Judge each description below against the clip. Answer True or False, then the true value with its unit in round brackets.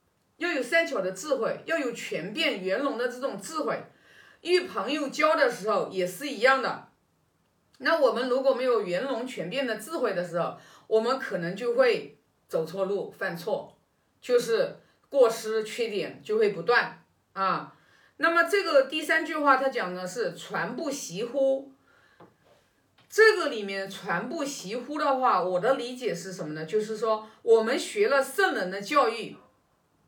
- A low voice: False (265 Hz)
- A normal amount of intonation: False (6.8 semitones)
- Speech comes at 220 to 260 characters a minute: True (230 characters per minute)